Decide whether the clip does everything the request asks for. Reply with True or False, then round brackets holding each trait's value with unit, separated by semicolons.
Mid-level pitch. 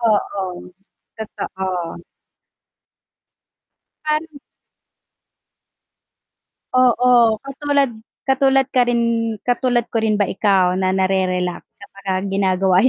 False (215 Hz)